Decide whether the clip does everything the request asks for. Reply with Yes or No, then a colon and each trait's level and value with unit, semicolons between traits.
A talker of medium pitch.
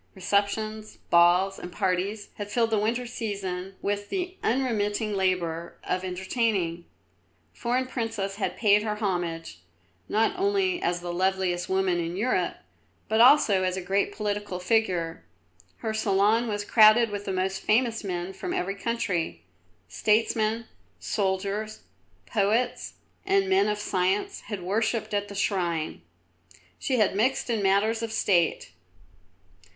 No: high, 205 Hz